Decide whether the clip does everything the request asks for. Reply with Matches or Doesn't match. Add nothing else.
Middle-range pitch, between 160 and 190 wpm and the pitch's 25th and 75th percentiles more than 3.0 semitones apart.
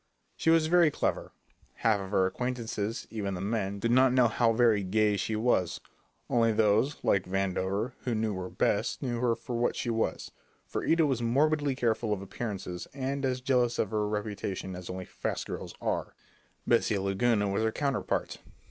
Doesn't match